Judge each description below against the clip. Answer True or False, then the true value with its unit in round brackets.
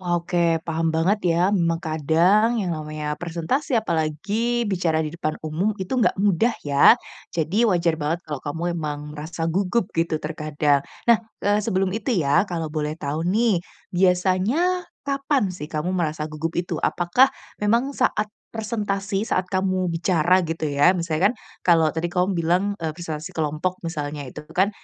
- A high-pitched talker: False (175 Hz)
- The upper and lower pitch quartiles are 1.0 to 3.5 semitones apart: False (4.1 semitones)